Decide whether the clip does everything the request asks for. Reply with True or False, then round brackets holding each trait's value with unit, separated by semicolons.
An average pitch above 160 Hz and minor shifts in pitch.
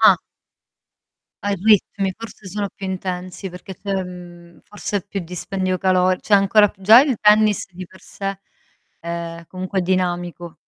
True (190 Hz; 2.2 semitones)